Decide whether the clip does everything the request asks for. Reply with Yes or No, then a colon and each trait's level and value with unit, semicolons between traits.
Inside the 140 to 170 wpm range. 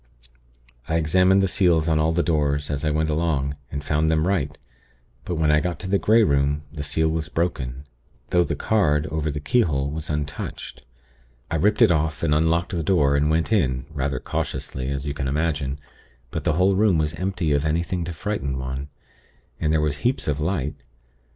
No: average, 195 wpm